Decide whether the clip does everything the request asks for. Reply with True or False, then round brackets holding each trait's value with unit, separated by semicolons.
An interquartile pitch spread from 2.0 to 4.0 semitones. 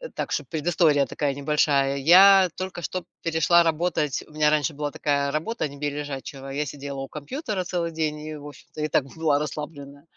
True (2.7 semitones)